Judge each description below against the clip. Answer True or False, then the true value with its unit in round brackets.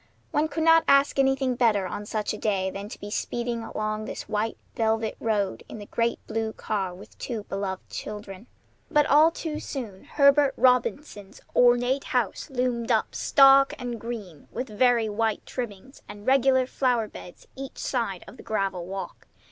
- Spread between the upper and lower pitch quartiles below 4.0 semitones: False (4.3 semitones)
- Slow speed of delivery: False (170 wpm)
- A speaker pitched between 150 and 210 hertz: False (230 Hz)